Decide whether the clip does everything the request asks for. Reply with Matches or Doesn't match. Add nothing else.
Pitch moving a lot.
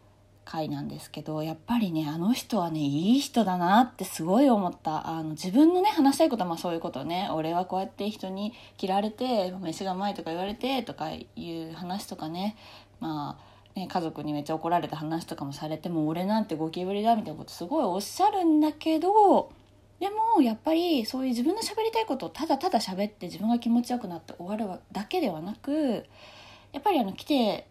Matches